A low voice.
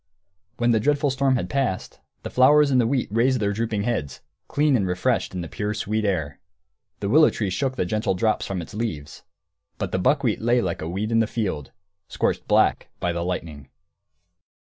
Yes: low, 110 Hz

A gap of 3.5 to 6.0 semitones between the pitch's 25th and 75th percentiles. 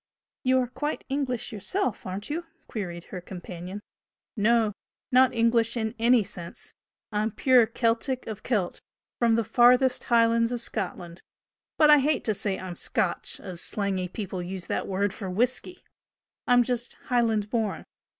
Yes: average, 4.1 semitones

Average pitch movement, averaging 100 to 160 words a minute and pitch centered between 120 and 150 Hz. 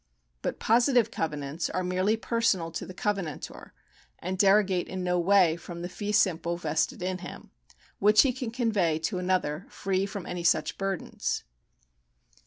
No: average, 3.3 semitones; average, 155 wpm; medium, 185 Hz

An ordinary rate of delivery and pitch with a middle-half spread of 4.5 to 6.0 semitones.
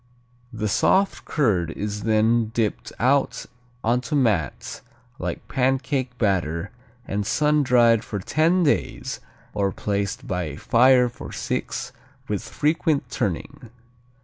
No: slow, 120 wpm; average, 4.9 semitones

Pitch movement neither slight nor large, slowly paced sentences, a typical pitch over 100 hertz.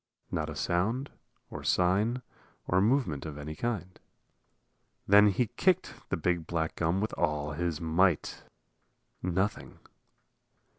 No: average, 4.6 semitones; slow, 120 wpm; very low, 90 Hz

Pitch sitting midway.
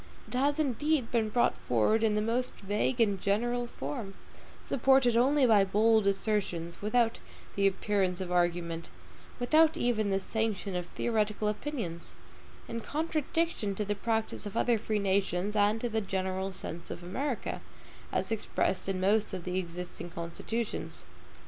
No: high, 210 Hz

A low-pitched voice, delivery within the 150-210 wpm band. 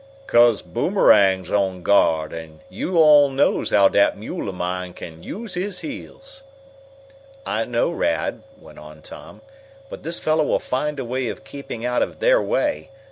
Yes: low, 120 Hz; average, 165 wpm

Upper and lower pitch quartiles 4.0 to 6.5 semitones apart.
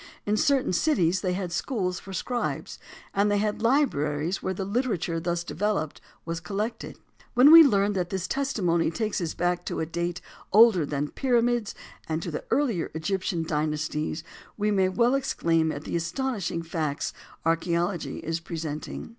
Yes: average, 4.6 semitones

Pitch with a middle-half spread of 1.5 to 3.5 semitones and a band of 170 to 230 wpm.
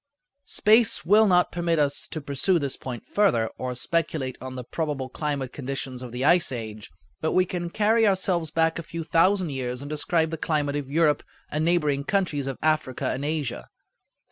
No: average, 4.4 semitones; average, 185 wpm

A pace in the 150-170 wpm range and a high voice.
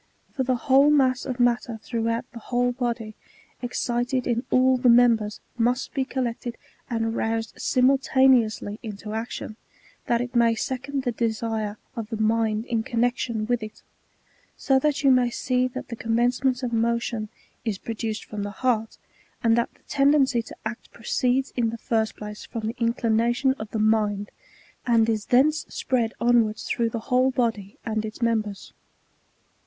Yes: average, 165 wpm; high, 235 Hz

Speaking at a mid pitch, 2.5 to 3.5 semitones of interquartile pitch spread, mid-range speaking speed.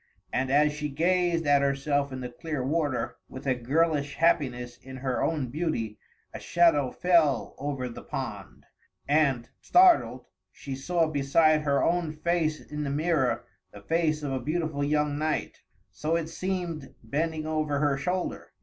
Yes: medium, 150 Hz; average, 3.1 semitones; average, 160 wpm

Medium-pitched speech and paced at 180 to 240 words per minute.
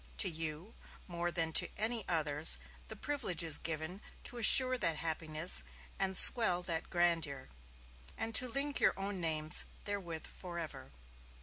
No: medium, 175 Hz; average, 140 wpm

